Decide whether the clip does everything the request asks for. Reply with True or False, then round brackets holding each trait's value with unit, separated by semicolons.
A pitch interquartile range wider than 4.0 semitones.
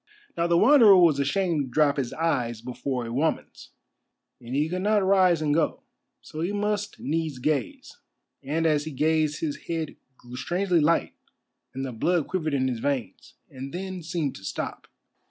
True (4.5 semitones)